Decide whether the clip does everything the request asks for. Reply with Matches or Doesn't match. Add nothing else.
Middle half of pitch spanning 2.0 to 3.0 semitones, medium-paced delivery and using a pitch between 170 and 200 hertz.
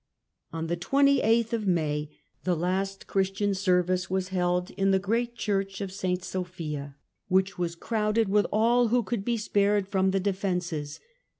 Matches